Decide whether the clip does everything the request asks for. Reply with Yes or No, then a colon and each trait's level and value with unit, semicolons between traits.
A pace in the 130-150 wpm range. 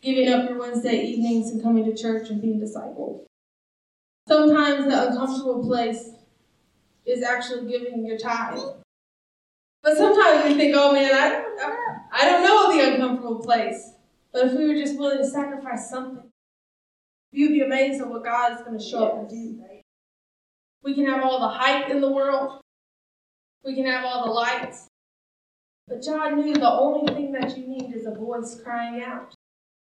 No: average, 175 wpm